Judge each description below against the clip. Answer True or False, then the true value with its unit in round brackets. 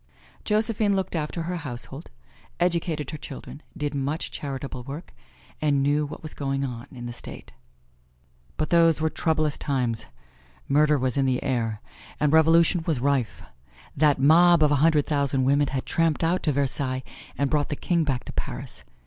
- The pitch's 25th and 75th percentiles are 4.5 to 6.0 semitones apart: False (3.0 semitones)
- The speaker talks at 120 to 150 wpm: False (170 wpm)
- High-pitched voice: False (145 Hz)